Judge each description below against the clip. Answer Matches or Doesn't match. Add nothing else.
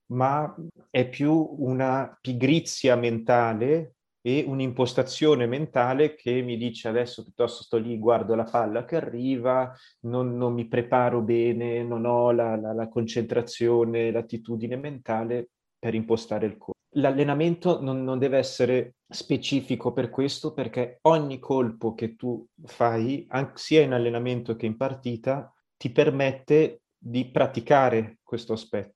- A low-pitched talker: Matches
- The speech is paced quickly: Doesn't match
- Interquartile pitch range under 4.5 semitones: Matches